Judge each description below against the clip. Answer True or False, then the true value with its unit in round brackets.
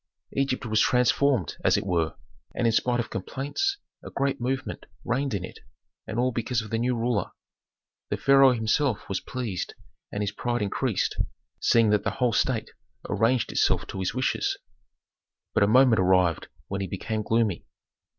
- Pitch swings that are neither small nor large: True (3.9 semitones)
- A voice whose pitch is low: True (115 Hz)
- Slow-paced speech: False (170 wpm)